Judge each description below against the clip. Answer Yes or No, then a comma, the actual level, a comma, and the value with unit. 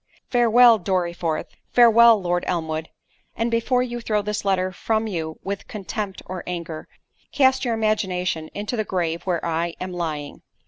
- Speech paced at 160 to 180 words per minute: No, average, 140 wpm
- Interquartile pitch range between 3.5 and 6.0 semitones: Yes, average, 4.7 semitones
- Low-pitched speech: No, high, 190 Hz